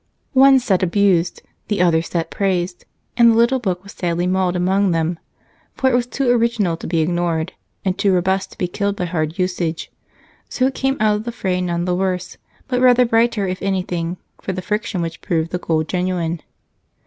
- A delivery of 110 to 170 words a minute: No, average, 195 wpm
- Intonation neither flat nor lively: Yes, average, 3.7 semitones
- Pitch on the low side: No, medium, 185 Hz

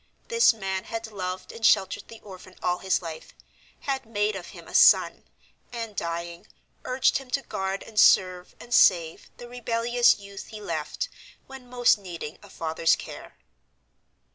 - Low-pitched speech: No, high, 205 Hz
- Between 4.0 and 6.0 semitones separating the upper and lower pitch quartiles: Yes, average, 4.5 semitones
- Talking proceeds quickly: No, average, 160 wpm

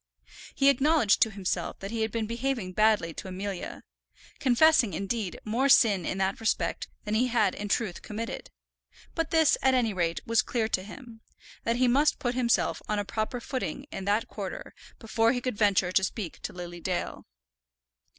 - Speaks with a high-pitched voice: Yes, high, 220 Hz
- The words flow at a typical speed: Yes, average, 180 wpm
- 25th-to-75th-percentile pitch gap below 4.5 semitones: Yes, average, 4.1 semitones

